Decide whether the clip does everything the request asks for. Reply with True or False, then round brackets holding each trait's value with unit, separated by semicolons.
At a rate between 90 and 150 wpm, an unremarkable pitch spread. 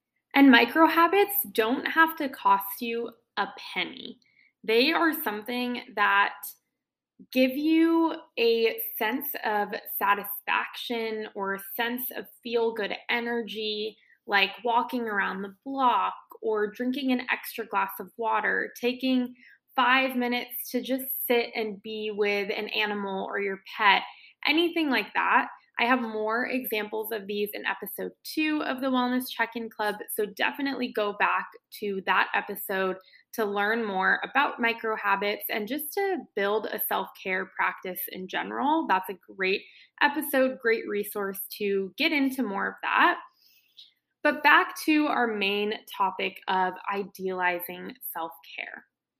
True (140 wpm; 4.6 semitones)